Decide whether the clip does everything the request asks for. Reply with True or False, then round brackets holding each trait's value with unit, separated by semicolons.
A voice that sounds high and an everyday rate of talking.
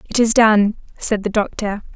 True (210 Hz; 185 wpm)